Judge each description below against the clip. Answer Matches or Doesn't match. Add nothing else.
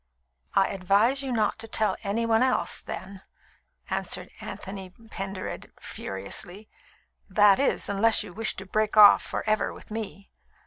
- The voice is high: Matches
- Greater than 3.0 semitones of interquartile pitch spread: Doesn't match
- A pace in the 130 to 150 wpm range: Matches